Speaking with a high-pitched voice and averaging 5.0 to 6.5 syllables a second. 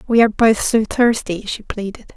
Yes: high, 215 Hz; 5.1 syllables/s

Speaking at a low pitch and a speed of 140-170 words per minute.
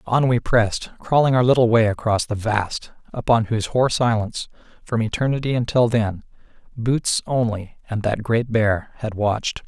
Yes: low, 115 Hz; average, 160 wpm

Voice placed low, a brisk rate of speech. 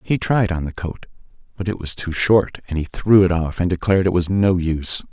Yes: very low, 90 Hz; fast, 245 wpm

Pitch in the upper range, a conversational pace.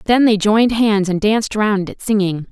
No: high, 210 Hz; fast, 215 wpm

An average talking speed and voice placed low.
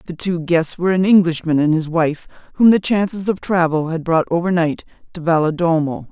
No: average, 195 wpm; medium, 170 Hz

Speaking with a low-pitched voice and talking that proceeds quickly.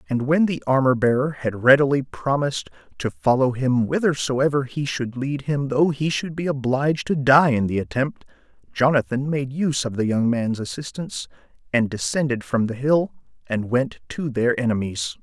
No: low, 130 Hz; average, 175 wpm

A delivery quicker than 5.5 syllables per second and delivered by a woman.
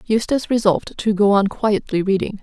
Yes: 5.7 syllables/s; female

